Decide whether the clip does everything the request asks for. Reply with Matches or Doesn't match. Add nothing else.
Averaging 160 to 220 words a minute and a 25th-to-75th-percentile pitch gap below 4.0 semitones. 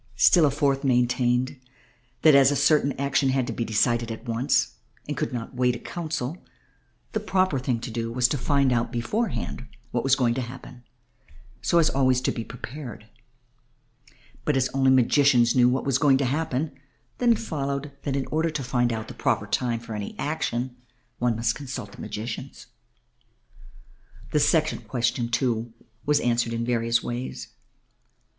Matches